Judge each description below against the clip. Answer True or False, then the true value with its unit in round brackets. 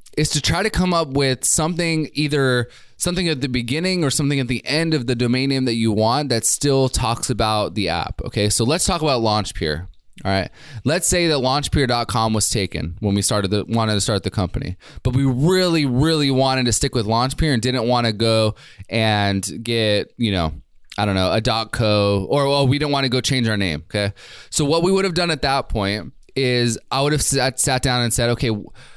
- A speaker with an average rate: False (225 wpm)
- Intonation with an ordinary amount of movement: True (4.9 semitones)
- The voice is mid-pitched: False (125 Hz)